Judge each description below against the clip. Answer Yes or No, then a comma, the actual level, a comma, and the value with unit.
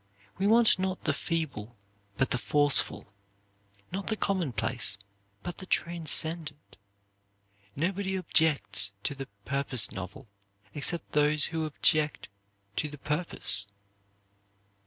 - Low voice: No, medium, 150 Hz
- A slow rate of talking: Yes, slow, 110 wpm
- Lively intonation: No, average, 4.5 semitones